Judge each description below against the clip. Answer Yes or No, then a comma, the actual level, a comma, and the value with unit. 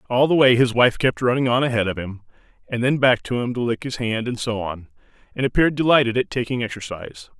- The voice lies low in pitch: Yes, low, 120 Hz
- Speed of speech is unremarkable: No, fast, 235 wpm